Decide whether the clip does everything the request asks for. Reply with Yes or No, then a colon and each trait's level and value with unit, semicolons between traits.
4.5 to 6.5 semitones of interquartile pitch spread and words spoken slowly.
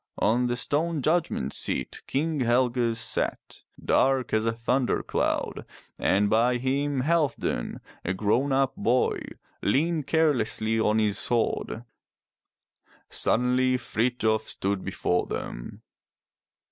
No: average, 3.7 semitones; slow, 110 wpm